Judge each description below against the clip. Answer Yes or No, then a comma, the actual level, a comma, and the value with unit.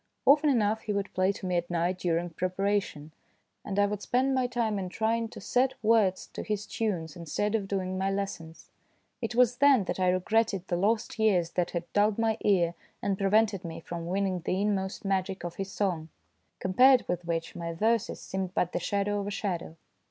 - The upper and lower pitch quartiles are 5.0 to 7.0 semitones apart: No, average, 3.5 semitones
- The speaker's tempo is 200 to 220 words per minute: Yes, fast, 205 wpm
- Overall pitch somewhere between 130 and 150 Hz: No, high, 195 Hz